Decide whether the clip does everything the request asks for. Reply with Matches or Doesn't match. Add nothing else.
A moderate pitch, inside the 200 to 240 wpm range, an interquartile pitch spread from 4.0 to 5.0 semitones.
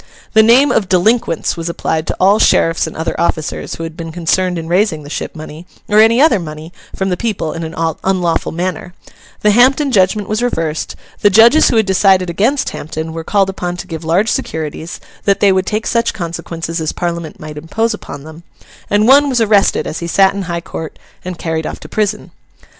Matches